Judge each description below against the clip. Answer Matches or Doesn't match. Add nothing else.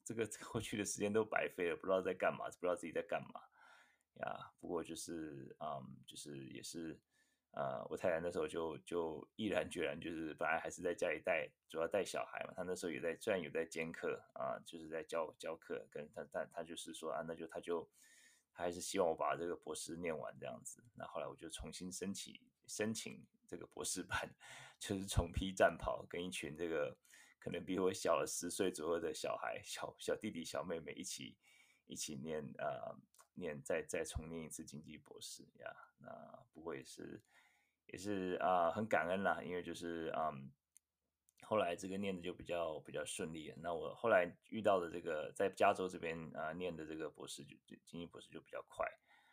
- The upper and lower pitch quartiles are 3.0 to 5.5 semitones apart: Matches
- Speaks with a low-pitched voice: Matches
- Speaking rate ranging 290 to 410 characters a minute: Matches